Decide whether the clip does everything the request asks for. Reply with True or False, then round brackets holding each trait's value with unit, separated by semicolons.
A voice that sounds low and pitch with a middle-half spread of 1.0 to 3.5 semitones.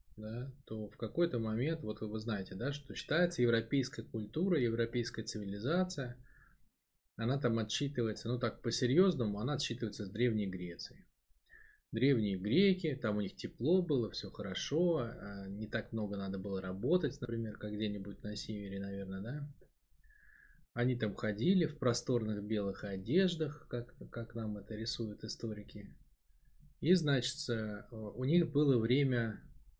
False (115 Hz; 4.9 semitones)